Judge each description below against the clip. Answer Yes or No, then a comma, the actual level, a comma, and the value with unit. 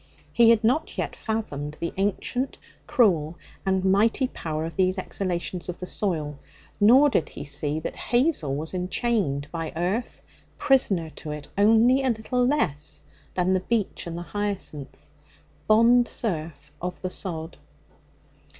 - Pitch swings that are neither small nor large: No, wide, 6.1 semitones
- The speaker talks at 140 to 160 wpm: Yes, average, 145 wpm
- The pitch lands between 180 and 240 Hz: Yes, medium, 185 Hz